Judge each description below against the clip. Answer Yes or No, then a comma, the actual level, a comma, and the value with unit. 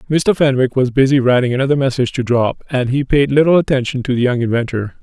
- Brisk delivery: Yes, fast, 215 wpm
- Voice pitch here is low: Yes, low, 130 Hz